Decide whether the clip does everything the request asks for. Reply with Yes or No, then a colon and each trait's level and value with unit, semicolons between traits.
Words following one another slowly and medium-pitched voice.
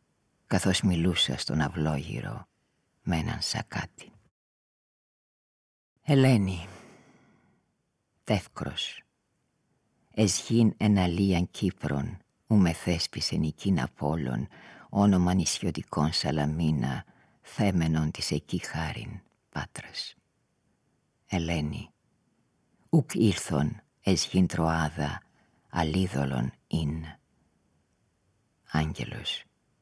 No: slow, 65 wpm; very low, 85 Hz